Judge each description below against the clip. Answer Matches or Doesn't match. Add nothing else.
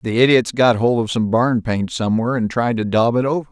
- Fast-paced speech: Matches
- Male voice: Matches